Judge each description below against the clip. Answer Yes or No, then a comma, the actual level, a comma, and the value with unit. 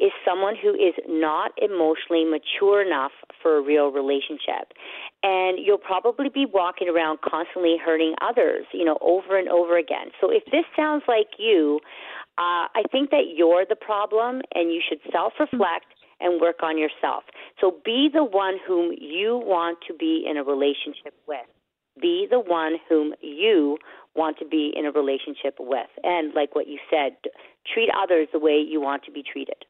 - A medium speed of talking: Yes, average, 180 wpm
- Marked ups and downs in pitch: Yes, wide, 8.0 semitones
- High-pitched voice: No, medium, 175 Hz